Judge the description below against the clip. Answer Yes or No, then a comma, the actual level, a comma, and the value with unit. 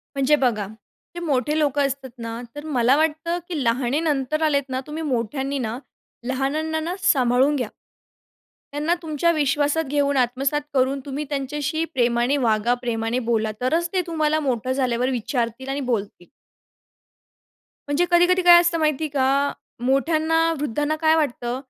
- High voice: Yes, very high, 280 Hz